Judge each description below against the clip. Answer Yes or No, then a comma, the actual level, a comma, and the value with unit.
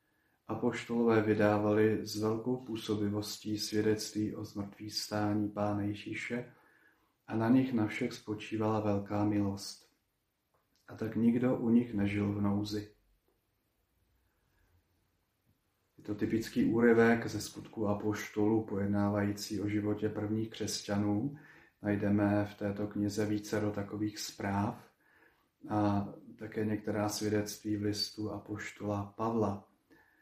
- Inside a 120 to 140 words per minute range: No, slow, 110 wpm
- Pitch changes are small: Yes, narrow, 1.2 semitones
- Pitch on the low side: Yes, low, 105 Hz